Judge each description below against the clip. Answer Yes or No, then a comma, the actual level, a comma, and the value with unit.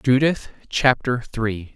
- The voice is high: No, low, 125 Hz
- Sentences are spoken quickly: No, slow, 105 wpm